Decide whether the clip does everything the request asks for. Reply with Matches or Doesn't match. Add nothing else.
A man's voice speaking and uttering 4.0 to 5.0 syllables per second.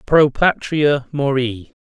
Doesn't match